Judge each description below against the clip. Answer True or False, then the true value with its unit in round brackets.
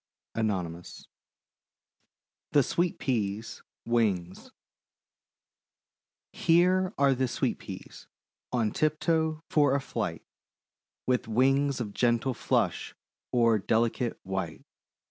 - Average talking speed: False (85 wpm)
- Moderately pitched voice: False (125 Hz)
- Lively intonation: False (4.6 semitones)